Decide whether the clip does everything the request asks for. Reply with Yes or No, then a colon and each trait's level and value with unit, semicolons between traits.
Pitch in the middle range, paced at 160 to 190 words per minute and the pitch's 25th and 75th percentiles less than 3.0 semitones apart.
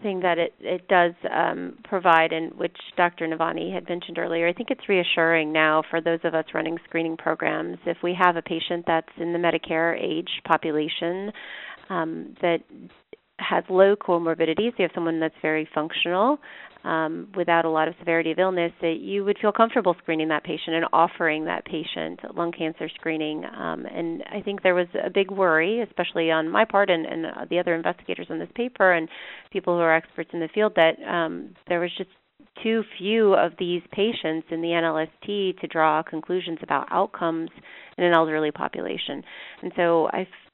Yes: medium, 170 Hz; average, 185 wpm; narrow, 2.5 semitones